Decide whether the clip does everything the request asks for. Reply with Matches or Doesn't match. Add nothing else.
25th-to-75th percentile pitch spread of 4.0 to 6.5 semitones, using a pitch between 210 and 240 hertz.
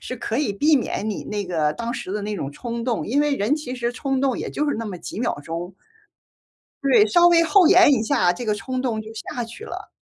Matches